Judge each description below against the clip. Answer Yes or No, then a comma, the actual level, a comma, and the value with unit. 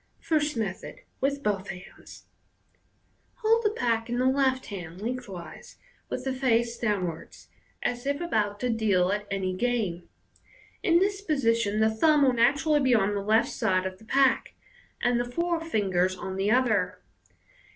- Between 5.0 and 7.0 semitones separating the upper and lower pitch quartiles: Yes, average, 5.3 semitones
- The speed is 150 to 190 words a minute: Yes, average, 160 wpm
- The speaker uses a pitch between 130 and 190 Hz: No, high, 230 Hz